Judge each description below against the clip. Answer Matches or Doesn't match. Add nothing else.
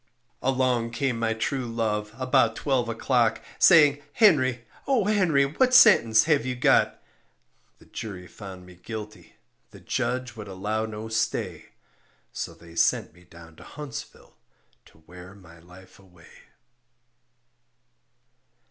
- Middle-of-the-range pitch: Doesn't match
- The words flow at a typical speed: Doesn't match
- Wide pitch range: Matches